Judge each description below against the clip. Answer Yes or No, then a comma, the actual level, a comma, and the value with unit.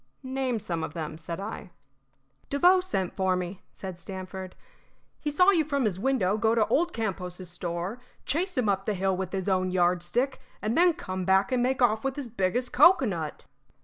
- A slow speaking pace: No, average, 185 wpm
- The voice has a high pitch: Yes, high, 200 Hz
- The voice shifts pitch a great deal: Yes, wide, 5.9 semitones